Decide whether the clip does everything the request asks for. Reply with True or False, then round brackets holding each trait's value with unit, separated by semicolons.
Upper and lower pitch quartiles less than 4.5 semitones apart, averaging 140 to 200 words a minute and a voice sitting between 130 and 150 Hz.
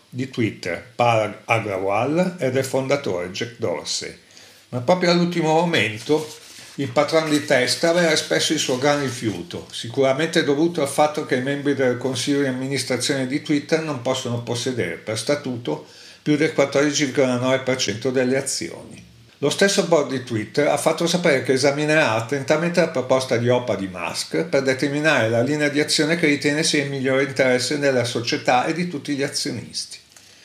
True (3.3 semitones; 160 wpm; 140 Hz)